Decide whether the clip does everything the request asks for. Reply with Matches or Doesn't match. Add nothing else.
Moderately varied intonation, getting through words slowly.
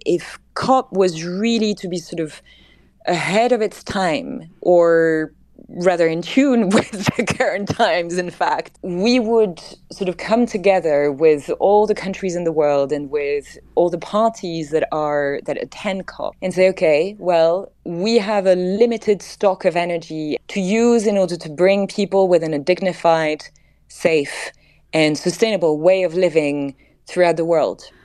Doesn't match